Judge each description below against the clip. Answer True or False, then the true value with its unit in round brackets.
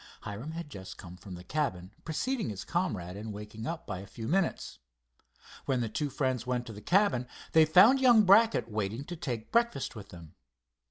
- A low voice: True (125 Hz)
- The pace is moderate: True (195 wpm)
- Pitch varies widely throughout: True (8.4 semitones)